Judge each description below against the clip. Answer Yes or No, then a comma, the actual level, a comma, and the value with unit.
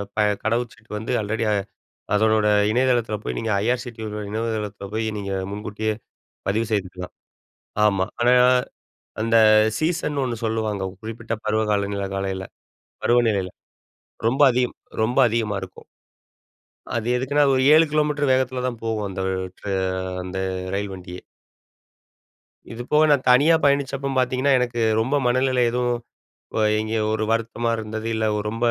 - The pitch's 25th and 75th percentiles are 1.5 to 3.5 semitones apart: Yes, average, 3.0 semitones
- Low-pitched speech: Yes, low, 115 Hz